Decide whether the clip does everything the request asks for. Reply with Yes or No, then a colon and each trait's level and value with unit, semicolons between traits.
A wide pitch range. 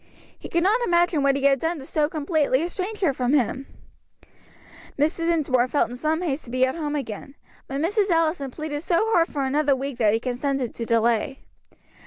No: average, 4.0 semitones